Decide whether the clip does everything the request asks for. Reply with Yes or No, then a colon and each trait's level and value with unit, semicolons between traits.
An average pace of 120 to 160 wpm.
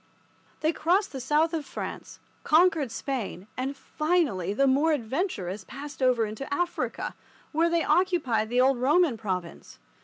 Yes: average, 145 wpm